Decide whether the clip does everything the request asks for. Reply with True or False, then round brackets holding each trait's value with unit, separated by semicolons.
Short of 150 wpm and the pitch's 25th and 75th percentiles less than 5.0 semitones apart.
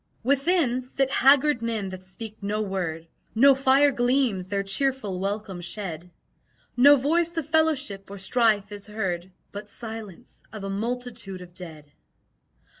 False (140 wpm; 5.4 semitones)